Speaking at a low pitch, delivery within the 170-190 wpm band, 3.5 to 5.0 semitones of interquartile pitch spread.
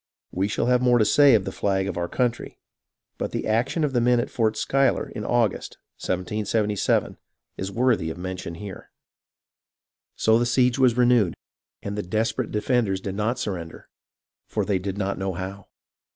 Yes: low, 105 Hz; average, 175 wpm; average, 4.0 semitones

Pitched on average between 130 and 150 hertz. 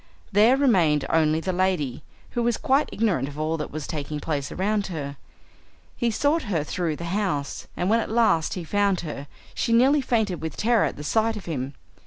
No: medium, 185 Hz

